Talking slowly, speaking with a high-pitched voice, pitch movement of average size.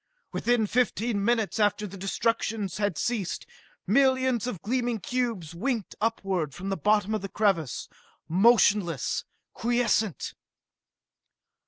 Yes: slow, 115 wpm; high, 215 Hz; average, 3.6 semitones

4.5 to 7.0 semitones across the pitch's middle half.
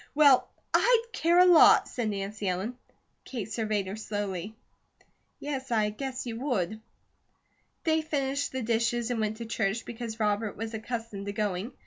No: average, 3.9 semitones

